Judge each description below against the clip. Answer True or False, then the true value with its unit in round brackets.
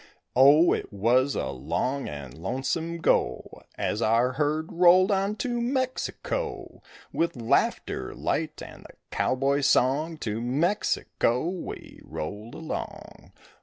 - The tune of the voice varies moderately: False (6.3 semitones)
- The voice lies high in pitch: False (140 Hz)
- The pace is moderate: False (120 wpm)